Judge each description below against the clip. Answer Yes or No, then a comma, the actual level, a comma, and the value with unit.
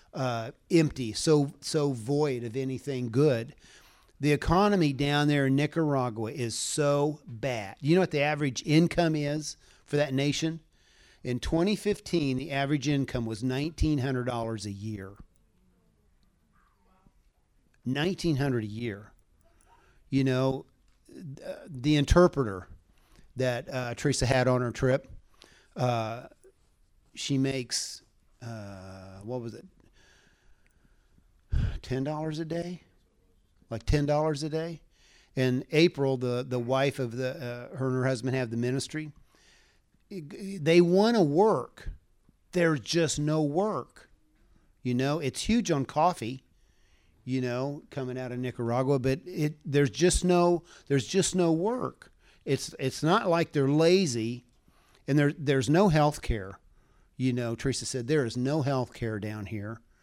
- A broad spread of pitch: No, average, 4.3 semitones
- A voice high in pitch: No, low, 135 Hz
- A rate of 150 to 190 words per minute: No, slow, 135 wpm